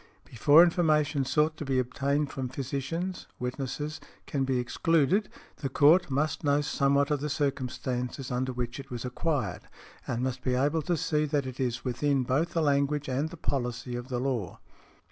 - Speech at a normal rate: Yes, average, 175 wpm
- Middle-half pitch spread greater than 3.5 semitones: No, average, 2.9 semitones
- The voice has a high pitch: No, medium, 140 Hz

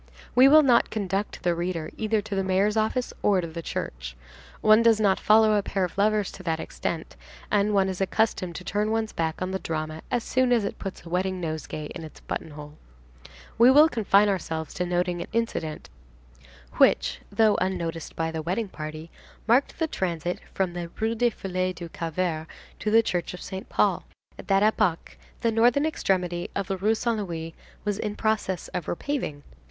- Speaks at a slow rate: No, average, 190 wpm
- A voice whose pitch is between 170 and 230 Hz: Yes, high, 190 Hz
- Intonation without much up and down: No, average, 4.3 semitones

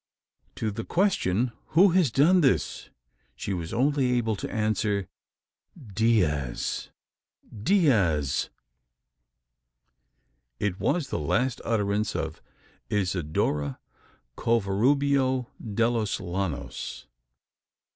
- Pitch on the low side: Yes, low, 110 Hz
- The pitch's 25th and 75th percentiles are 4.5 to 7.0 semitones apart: Yes, wide, 5.5 semitones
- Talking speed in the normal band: No, slow, 85 wpm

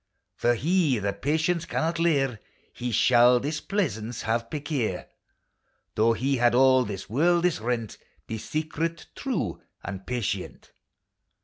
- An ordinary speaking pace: No, slow, 125 wpm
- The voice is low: Yes, low, 130 Hz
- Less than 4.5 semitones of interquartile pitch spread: No, wide, 5.6 semitones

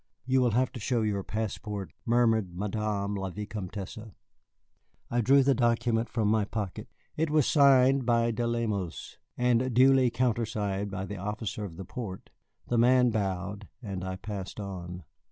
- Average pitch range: Yes, average, 3.5 semitones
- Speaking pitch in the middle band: No, low, 110 Hz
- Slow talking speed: No, average, 155 wpm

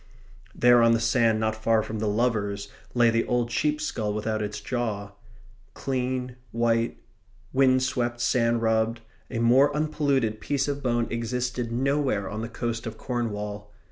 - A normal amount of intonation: No, narrow, 2.2 semitones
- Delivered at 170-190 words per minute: No, average, 155 wpm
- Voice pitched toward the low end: Yes, low, 115 Hz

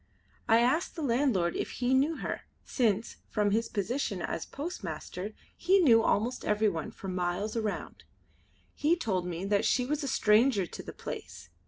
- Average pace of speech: Yes, average, 165 wpm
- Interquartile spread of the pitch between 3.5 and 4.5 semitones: No, average, 5.1 semitones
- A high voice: Yes, high, 225 Hz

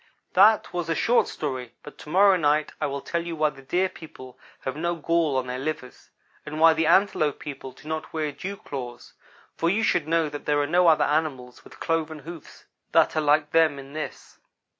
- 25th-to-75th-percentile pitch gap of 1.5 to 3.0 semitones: Yes, average, 2.7 semitones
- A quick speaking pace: Yes, fast, 210 wpm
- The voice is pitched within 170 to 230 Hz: No, medium, 155 Hz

